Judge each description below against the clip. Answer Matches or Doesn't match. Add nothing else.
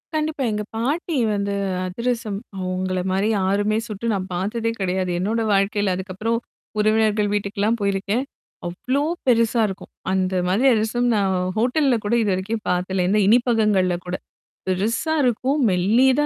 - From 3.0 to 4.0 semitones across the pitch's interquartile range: Matches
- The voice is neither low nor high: Doesn't match